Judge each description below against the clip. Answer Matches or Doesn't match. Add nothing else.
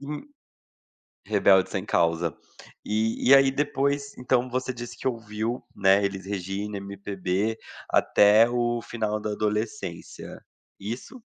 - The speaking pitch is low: Matches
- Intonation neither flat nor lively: Matches